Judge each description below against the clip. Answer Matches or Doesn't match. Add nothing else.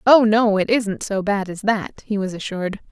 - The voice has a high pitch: Matches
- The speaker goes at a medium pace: Doesn't match